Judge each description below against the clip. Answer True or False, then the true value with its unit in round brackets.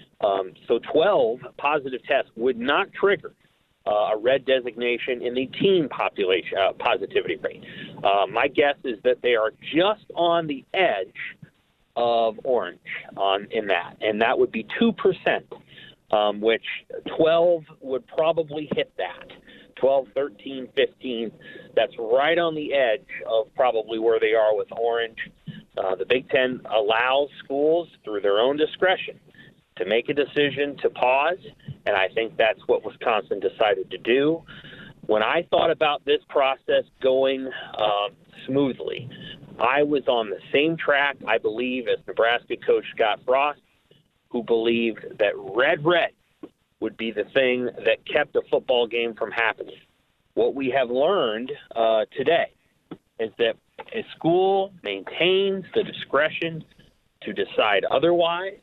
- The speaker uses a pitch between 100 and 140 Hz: False (150 Hz)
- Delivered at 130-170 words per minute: True (145 wpm)